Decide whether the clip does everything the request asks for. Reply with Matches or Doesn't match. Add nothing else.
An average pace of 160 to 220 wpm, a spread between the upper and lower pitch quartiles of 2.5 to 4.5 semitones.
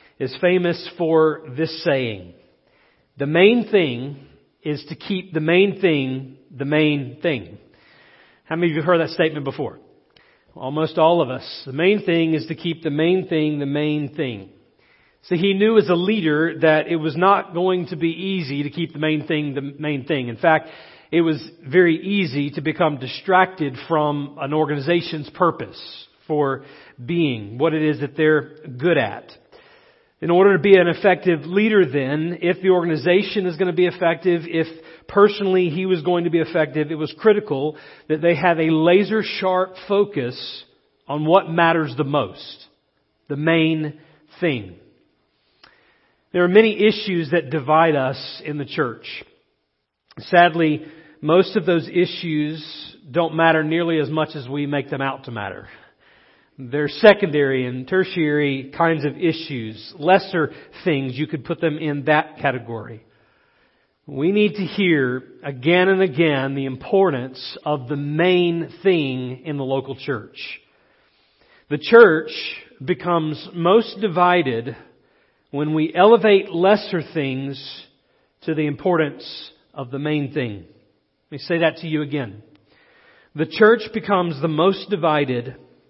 Doesn't match